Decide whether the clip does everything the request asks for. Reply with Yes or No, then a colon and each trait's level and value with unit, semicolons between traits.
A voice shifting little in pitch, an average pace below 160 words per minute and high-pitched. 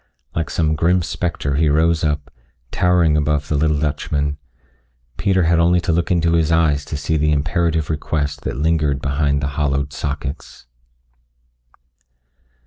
No: narrow, 2.3 semitones; average, 145 wpm; very low, 75 Hz